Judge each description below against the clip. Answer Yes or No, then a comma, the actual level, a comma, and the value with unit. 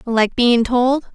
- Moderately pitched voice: No, high, 240 Hz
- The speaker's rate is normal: Yes, average, 160 wpm